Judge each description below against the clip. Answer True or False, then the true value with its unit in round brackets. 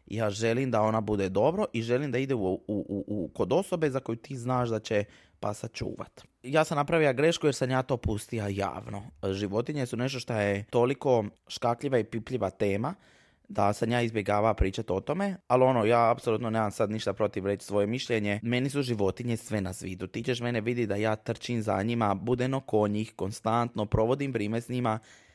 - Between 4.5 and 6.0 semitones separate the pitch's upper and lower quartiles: False (3.4 semitones)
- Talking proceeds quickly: True (200 wpm)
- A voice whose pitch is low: True (115 Hz)